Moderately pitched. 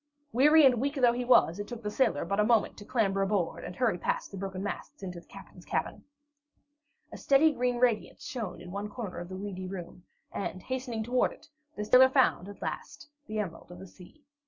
No: high, 210 Hz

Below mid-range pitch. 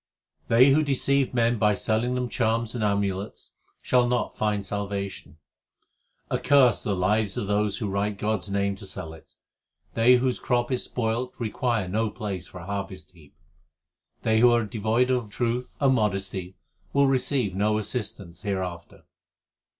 Yes: low, 110 Hz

